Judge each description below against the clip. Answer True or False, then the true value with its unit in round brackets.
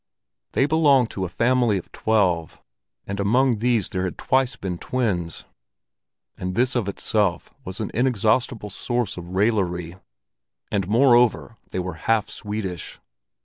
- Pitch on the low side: True (105 Hz)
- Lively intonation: False (4.7 semitones)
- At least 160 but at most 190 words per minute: False (140 wpm)